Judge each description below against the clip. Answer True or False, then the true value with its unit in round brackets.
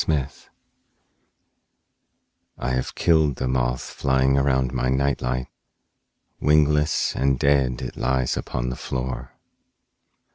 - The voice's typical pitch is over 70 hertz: False (65 Hz)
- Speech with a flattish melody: True (1.8 semitones)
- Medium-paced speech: False (115 wpm)